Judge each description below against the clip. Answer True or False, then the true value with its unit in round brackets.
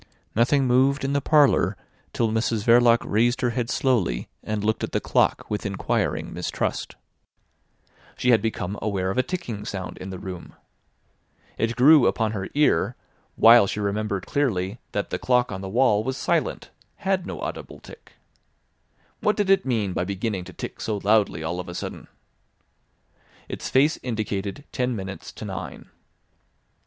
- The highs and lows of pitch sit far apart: False (4.3 semitones)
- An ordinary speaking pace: True (165 wpm)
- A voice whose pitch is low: True (110 Hz)